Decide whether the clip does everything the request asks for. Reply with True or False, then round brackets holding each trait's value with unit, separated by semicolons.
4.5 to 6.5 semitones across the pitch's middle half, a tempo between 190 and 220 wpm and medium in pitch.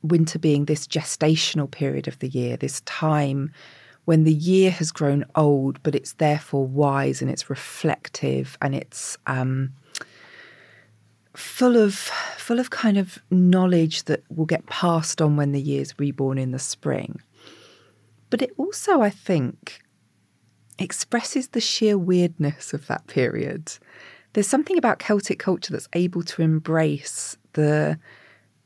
False (5.2 semitones; 140 wpm; 155 Hz)